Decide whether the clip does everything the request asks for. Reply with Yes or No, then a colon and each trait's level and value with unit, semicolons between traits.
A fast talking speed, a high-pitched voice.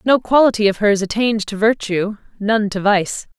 No: average, 175 wpm; high, 210 Hz